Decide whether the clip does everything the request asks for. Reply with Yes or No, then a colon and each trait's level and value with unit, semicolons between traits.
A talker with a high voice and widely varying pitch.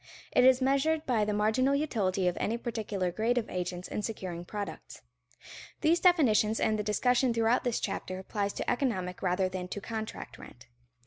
No: high, 215 Hz; average, 4.7 semitones